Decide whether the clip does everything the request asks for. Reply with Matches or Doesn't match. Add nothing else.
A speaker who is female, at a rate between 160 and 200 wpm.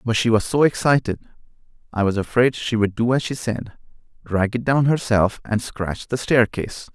Doesn't match